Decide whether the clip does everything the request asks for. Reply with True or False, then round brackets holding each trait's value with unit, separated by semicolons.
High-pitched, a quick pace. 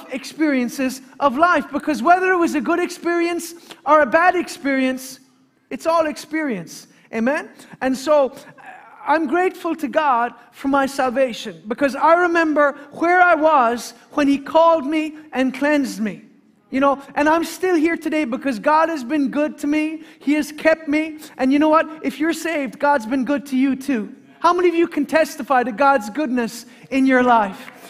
False (290 Hz; 180 wpm)